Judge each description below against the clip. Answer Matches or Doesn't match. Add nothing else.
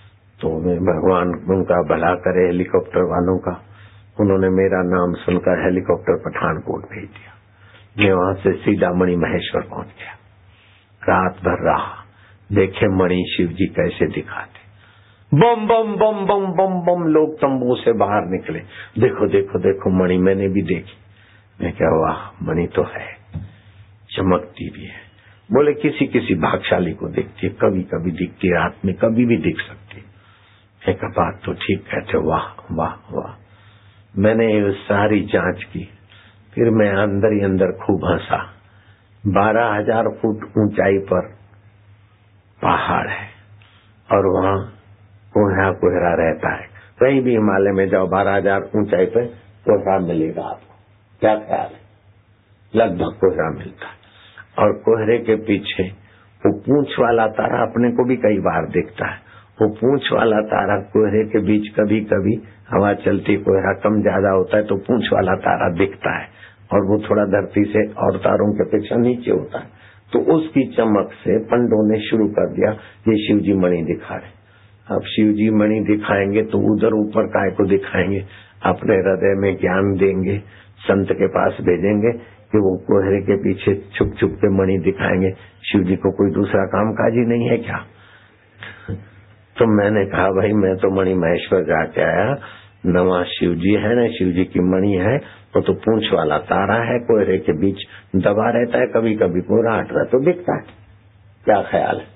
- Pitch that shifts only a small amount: Matches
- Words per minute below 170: Matches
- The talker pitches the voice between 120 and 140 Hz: Doesn't match